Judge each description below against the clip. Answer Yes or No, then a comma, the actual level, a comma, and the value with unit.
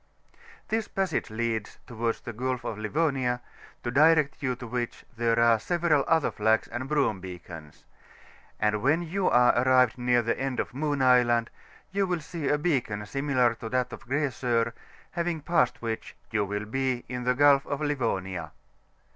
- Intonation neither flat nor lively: Yes, average, 4.1 semitones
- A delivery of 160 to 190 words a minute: Yes, average, 165 wpm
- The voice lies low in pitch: Yes, low, 125 Hz